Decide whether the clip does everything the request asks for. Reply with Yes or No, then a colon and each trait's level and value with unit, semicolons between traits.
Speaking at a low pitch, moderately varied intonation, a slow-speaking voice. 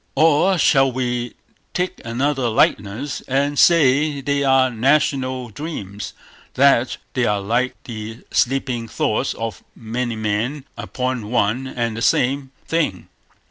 Yes: low, 130 Hz; average, 3.4 semitones; slow, 125 wpm